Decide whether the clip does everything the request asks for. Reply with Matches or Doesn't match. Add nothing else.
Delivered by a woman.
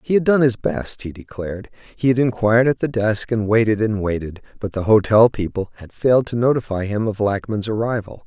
Doesn't match